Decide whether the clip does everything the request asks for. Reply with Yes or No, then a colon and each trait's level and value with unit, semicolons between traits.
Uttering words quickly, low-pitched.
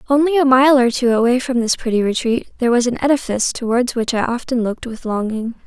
No: fast, 220 wpm; high, 245 Hz